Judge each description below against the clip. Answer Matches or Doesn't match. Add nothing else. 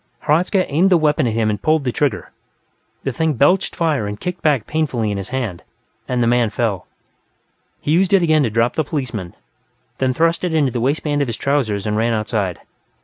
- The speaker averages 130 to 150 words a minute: Doesn't match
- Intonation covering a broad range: Matches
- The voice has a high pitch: Doesn't match